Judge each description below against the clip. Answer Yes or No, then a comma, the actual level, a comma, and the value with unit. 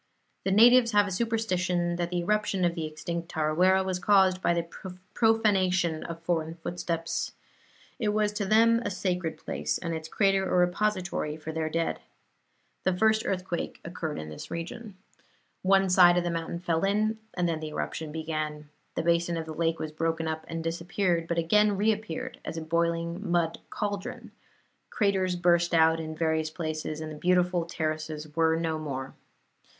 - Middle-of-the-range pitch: Yes, medium, 175 Hz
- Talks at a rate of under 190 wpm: Yes, average, 170 wpm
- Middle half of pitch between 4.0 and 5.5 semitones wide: No, average, 3.0 semitones